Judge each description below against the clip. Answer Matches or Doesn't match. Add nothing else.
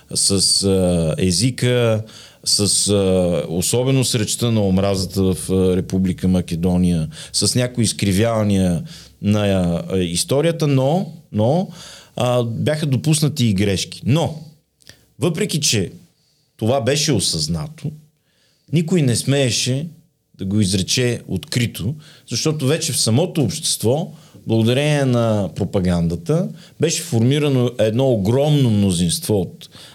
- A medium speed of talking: Doesn't match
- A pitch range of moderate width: Doesn't match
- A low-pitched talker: Matches